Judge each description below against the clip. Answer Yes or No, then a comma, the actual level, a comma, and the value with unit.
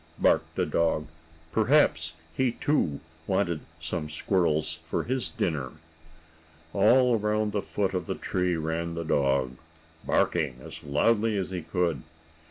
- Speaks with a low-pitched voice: Yes, very low, 85 Hz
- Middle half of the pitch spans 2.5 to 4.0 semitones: No, average, 5.1 semitones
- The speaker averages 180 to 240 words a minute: No, average, 145 wpm